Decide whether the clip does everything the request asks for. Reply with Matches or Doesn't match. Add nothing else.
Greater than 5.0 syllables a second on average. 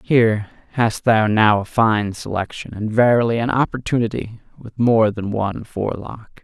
Doesn't match